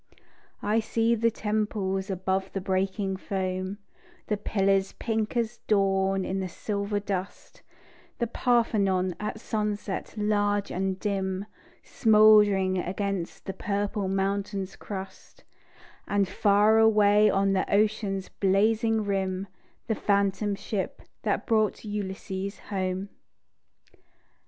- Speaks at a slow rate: Yes, slow, 110 wpm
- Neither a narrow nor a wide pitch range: No, narrow, 1.7 semitones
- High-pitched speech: Yes, high, 200 Hz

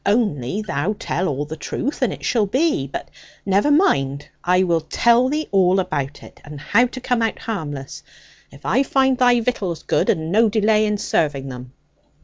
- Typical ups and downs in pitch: No, wide, 8.2 semitones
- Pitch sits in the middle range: No, high, 200 Hz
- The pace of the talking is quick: No, average, 185 wpm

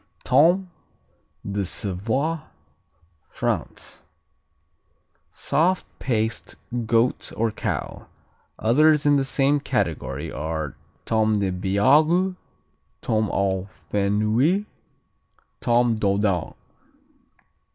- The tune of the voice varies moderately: No, wide, 6.5 semitones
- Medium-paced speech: No, slow, 80 wpm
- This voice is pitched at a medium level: No, low, 115 Hz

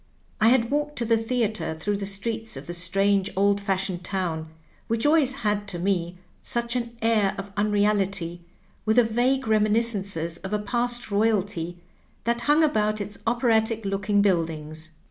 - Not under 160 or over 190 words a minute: Yes, average, 165 wpm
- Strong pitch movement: No, average, 3.3 semitones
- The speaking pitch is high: Yes, high, 205 Hz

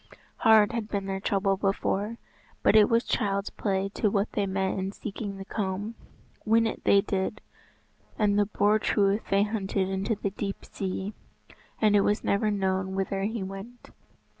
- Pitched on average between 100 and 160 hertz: No, high, 200 Hz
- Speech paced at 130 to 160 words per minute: No, average, 170 wpm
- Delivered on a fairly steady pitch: Yes, narrow, 1.6 semitones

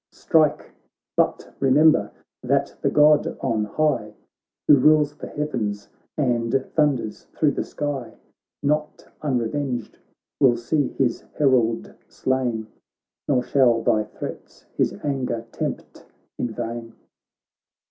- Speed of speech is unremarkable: No, slow, 110 wpm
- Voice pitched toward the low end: Yes, low, 130 Hz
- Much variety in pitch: No, average, 4.1 semitones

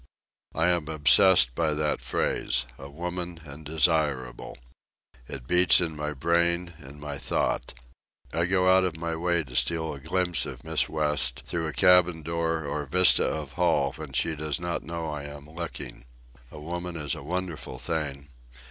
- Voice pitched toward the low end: Yes, very low, 80 Hz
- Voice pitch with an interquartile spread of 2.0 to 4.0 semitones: Yes, average, 3.0 semitones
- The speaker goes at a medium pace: Yes, average, 165 wpm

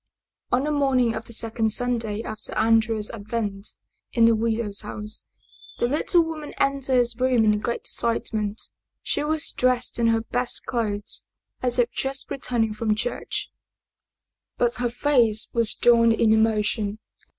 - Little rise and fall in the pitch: Yes, narrow, 2.2 semitones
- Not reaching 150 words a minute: No, average, 160 wpm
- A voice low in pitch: No, high, 230 Hz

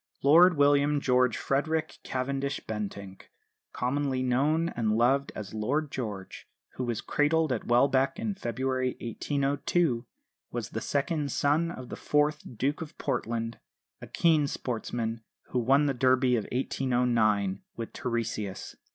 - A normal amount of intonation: Yes, average, 3.7 semitones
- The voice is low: Yes, low, 130 Hz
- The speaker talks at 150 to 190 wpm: No, slow, 135 wpm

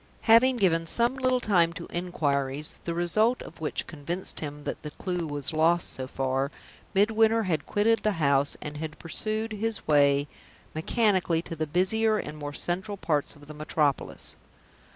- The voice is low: No, medium, 170 Hz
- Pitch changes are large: Yes, wide, 6.4 semitones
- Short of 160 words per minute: No, average, 165 wpm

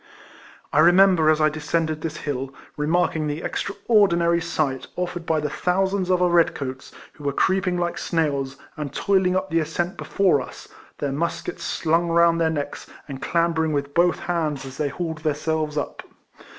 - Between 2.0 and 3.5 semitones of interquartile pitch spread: Yes, average, 2.9 semitones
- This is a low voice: No, medium, 165 Hz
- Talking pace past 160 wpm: Yes, average, 180 wpm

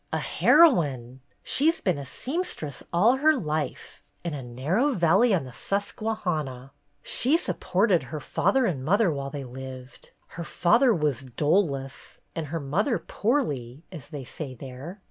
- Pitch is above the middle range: No, medium, 160 Hz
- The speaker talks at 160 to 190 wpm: No, average, 150 wpm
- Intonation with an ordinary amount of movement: No, wide, 7.7 semitones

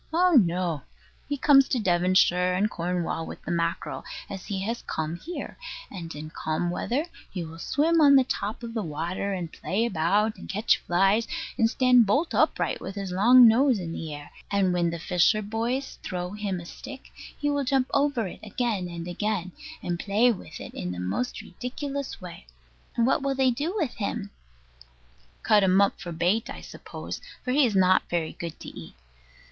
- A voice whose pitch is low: No, high, 200 Hz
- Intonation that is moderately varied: No, wide, 6.1 semitones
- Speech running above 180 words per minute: Yes, average, 190 wpm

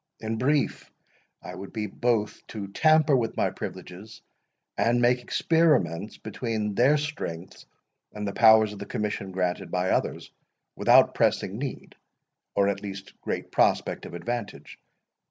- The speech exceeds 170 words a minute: No, average, 140 wpm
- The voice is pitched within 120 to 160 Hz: No, low, 105 Hz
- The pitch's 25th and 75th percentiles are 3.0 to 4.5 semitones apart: Yes, average, 3.8 semitones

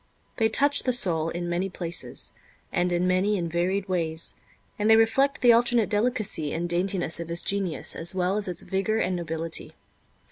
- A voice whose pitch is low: No, medium, 185 Hz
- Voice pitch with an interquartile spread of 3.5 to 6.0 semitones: Yes, average, 3.9 semitones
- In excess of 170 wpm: Yes, average, 180 wpm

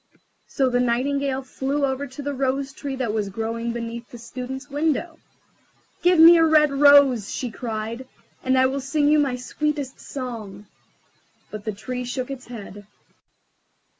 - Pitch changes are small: No, average, 3.2 semitones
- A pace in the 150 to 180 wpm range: Yes, average, 160 wpm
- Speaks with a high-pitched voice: Yes, very high, 260 Hz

